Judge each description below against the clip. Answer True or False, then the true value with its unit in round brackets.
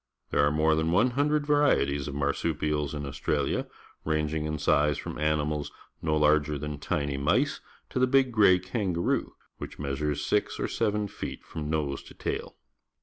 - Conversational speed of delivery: True (160 wpm)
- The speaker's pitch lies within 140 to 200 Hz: False (75 Hz)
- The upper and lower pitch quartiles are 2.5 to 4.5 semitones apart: True (4.1 semitones)